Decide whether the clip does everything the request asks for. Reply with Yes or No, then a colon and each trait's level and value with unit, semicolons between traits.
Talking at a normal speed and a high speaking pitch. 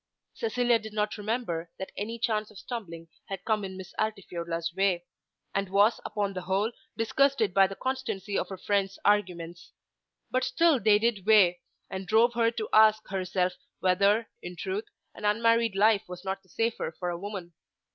Yes: average, 175 wpm; high, 205 Hz